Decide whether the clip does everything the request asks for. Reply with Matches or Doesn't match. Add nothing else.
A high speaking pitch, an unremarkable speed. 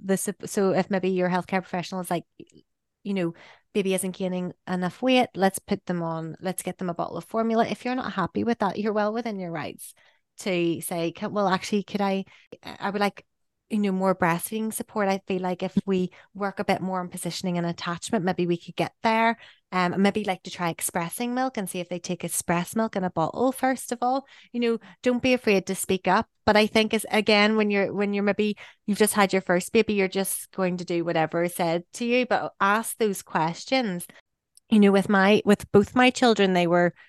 Doesn't match